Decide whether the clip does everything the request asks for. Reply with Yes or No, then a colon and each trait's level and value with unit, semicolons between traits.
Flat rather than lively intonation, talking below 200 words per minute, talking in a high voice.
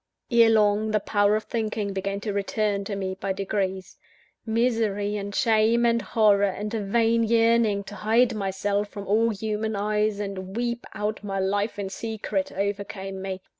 Yes: narrow, 1.9 semitones; average, 165 wpm; high, 210 Hz